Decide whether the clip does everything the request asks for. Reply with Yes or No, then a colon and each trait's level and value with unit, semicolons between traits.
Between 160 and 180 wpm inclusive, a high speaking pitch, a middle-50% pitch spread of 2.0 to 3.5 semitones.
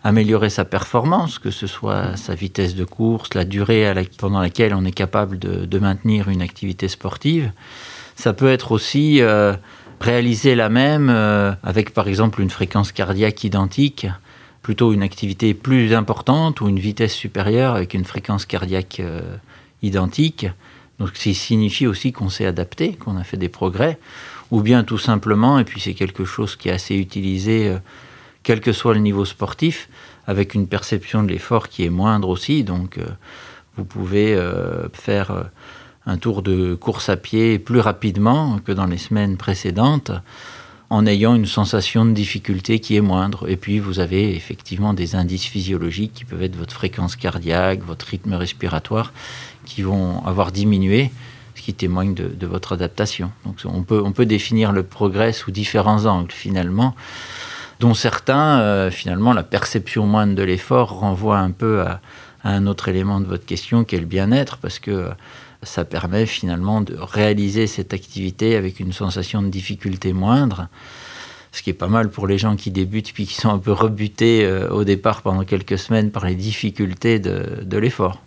No: average, 175 wpm; low, 105 Hz; average, 3.0 semitones